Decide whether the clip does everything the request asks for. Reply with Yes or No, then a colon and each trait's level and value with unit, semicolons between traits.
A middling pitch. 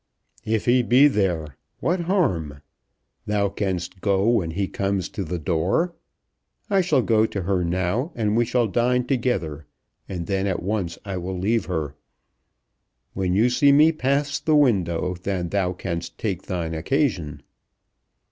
No: low, 100 Hz